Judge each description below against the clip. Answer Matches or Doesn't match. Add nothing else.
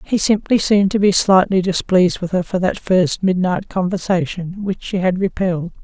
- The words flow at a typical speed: Matches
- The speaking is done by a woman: Matches